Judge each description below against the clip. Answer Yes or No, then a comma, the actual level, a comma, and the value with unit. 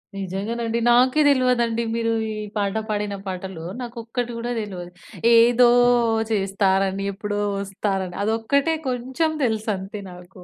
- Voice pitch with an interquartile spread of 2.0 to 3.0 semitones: No, average, 3.6 semitones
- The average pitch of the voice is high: Yes, high, 215 Hz